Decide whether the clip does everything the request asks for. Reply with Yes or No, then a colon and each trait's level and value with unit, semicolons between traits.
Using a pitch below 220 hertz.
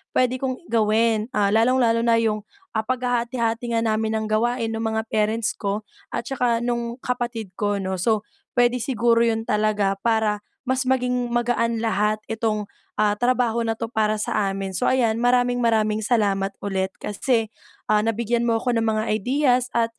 No: high, 230 Hz